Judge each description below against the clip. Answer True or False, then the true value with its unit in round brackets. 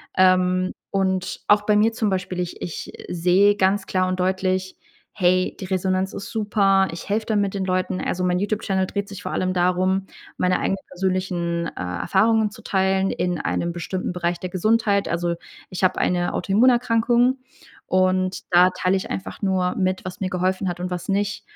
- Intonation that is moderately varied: False (1.6 semitones)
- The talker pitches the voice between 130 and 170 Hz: False (185 Hz)